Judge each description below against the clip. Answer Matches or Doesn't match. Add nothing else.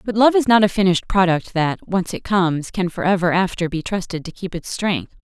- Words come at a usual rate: Doesn't match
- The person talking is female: Matches